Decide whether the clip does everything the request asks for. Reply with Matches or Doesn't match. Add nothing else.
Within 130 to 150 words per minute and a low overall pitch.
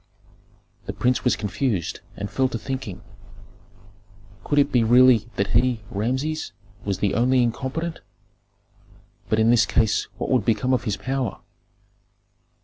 Matches